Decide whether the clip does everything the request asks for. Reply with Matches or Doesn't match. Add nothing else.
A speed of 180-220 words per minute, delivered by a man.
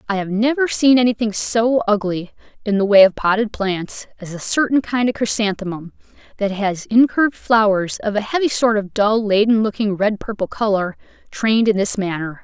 Doesn't match